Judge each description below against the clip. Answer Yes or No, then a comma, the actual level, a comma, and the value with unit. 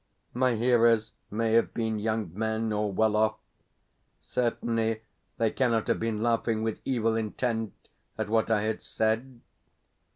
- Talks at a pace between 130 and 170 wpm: Yes, average, 140 wpm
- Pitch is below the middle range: Yes, low, 110 Hz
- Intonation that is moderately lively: No, narrow, 1.0 semitones